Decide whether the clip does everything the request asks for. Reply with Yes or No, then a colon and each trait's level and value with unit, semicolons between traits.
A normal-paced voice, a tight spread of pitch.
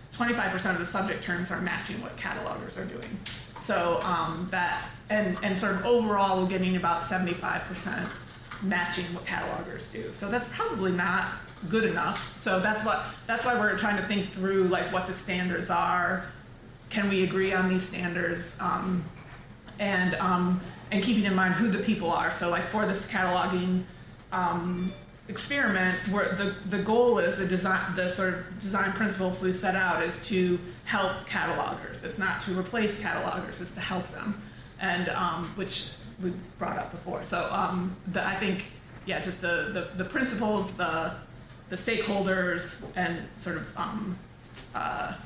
Yes: average, 165 wpm; narrow, 2.1 semitones